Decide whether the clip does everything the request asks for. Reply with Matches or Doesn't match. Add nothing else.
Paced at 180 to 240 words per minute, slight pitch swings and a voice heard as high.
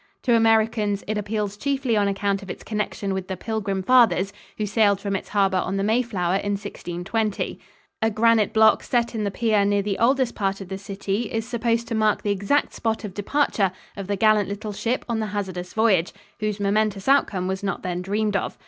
Matches